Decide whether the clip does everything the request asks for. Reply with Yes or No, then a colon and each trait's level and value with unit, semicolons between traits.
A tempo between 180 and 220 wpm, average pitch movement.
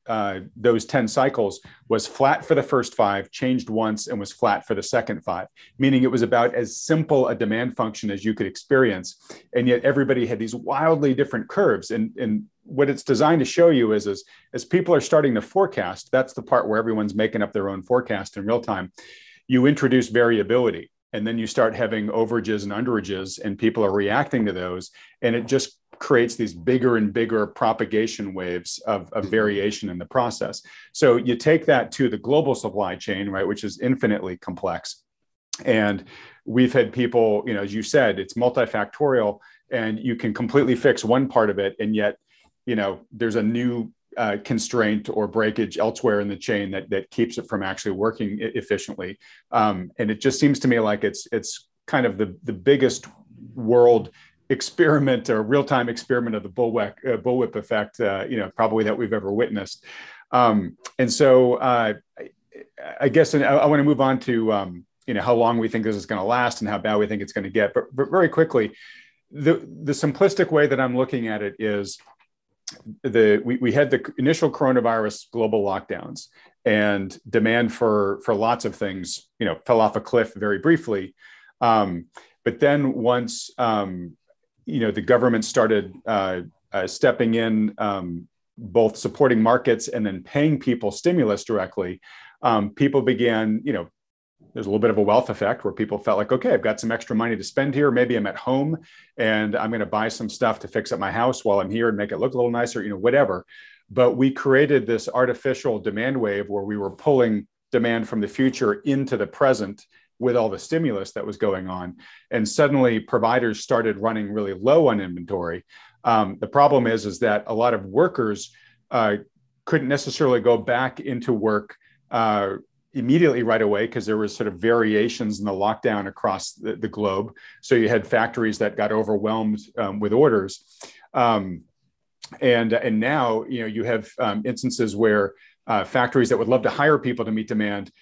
Yes: average, 195 wpm; average, 3.6 semitones